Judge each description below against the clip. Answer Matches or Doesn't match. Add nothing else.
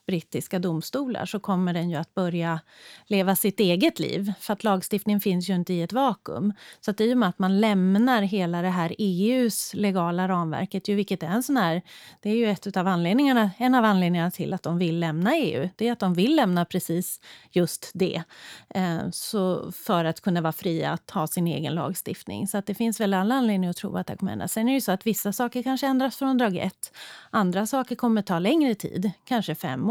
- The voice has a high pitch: Matches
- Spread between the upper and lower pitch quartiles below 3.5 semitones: Doesn't match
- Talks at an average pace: Doesn't match